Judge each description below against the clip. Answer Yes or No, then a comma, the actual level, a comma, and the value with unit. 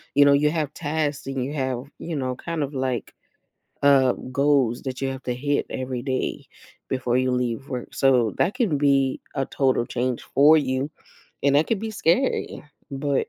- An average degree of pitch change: No, narrow, 2.3 semitones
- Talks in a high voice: No, low, 135 Hz